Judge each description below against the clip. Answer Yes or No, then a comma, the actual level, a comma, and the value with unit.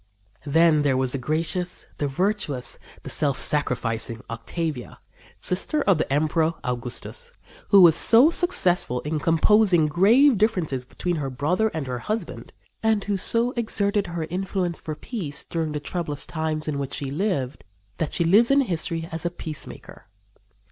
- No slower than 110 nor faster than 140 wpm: No, average, 155 wpm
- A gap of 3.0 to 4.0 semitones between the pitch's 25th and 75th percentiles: No, wide, 5.5 semitones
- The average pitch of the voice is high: No, medium, 165 Hz